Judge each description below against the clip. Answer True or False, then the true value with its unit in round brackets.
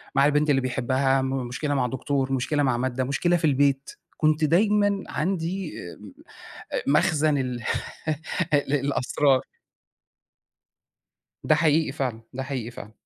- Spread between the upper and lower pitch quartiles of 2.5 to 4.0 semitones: True (2.8 semitones)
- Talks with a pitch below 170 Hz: True (140 Hz)